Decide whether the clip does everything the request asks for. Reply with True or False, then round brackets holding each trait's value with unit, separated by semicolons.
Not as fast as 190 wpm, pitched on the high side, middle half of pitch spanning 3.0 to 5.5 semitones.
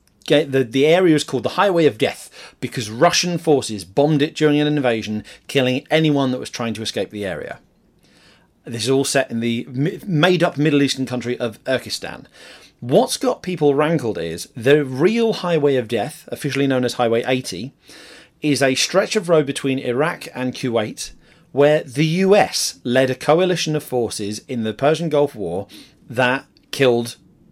False (170 wpm; 135 Hz; 3.9 semitones)